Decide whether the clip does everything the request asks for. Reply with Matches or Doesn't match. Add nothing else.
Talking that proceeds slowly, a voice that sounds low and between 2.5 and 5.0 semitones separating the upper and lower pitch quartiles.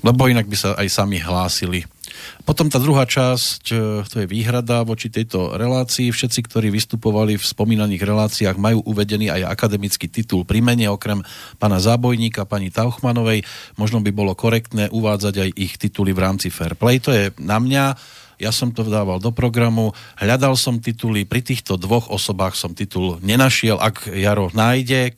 Doesn't match